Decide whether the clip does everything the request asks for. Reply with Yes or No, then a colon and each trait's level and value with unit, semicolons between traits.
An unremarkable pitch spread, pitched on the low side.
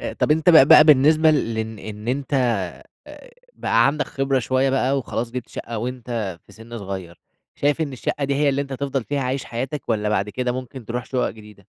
Yes: average, 3.7 semitones; low, 130 Hz